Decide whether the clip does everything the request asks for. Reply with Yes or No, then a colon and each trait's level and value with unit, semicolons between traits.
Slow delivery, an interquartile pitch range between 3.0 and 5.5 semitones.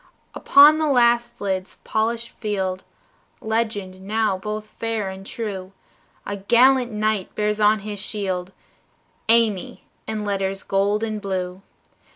No: slow, 125 wpm; narrow, 2.6 semitones